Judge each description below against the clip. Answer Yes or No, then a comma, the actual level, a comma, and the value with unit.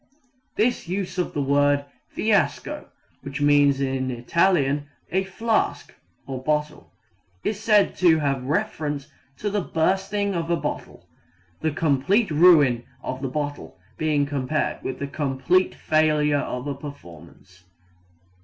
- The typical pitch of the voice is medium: Yes, medium, 150 Hz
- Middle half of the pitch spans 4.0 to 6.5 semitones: Yes, average, 4.6 semitones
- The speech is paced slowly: Yes, slow, 130 wpm